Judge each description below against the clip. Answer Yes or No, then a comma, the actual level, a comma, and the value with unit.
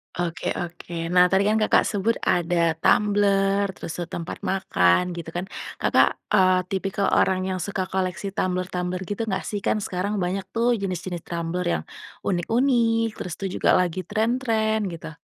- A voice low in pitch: No, high, 190 Hz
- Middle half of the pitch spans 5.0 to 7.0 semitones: No, average, 2.7 semitones